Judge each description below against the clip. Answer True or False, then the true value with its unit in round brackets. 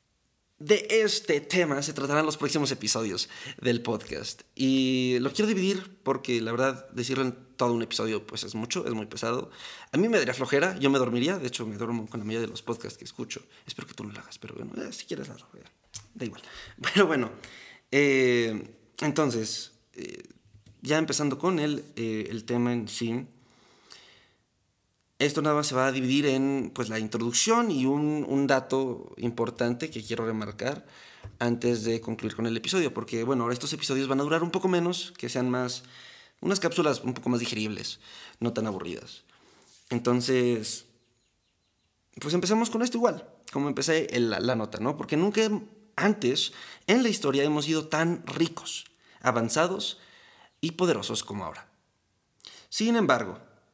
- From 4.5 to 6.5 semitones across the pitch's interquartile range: True (4.9 semitones)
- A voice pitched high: False (130 Hz)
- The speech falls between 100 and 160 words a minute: False (170 wpm)